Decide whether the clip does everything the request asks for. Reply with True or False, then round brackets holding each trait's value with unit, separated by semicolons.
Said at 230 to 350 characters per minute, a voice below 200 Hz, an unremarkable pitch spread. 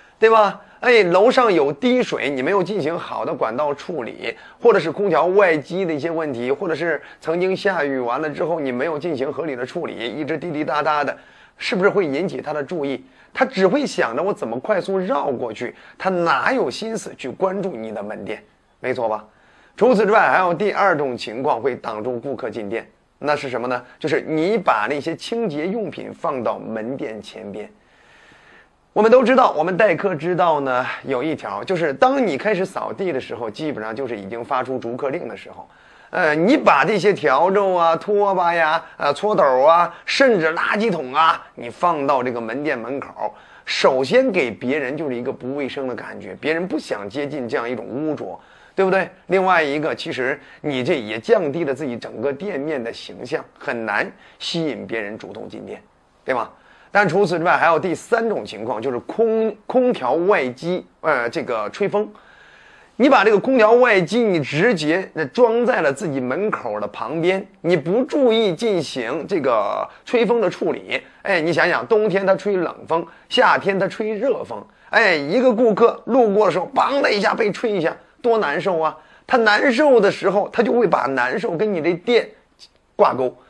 False (275 characters per minute; 190 Hz; 5.7 semitones)